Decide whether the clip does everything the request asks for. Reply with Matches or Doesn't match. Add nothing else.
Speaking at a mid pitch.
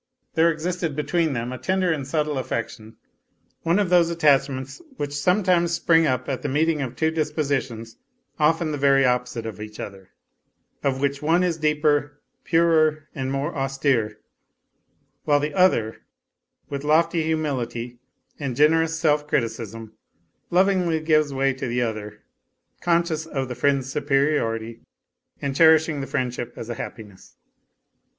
Matches